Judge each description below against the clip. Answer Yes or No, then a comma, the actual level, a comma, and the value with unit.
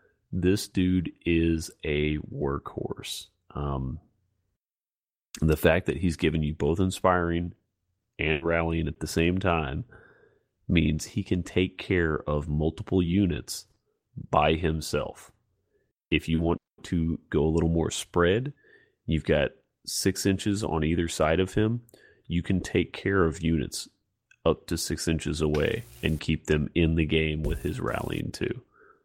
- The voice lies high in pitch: No, very low, 80 Hz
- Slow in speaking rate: No, average, 145 wpm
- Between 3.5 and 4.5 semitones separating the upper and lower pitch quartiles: No, average, 2.8 semitones